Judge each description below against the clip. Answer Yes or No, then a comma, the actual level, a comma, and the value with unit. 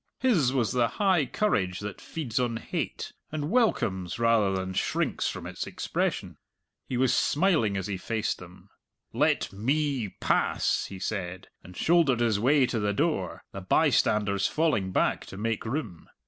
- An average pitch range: No, wide, 6.8 semitones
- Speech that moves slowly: No, average, 160 wpm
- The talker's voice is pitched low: Yes, low, 115 Hz